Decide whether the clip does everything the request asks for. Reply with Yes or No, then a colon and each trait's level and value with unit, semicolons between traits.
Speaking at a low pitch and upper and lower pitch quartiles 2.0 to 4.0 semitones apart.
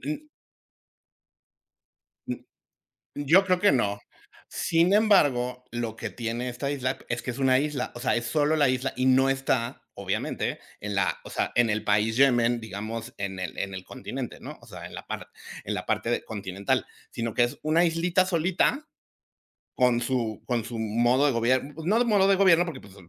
No: low, 125 Hz; average, 5.2 semitones